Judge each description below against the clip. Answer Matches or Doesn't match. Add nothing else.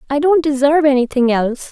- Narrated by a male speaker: Doesn't match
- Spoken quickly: Doesn't match